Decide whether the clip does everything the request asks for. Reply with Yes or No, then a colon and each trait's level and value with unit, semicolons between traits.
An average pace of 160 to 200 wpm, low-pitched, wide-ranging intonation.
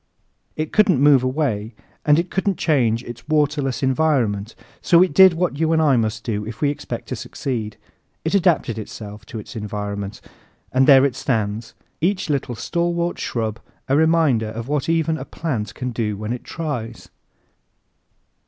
Yes: average, 165 wpm; low, 130 Hz; wide, 6.2 semitones